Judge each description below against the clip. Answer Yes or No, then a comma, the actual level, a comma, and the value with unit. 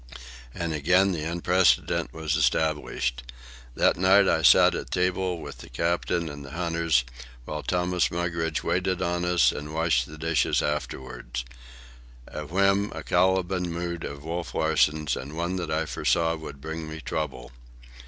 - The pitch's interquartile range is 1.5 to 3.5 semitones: Yes, average, 2.9 semitones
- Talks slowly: No, average, 145 wpm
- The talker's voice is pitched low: Yes, very low, 80 Hz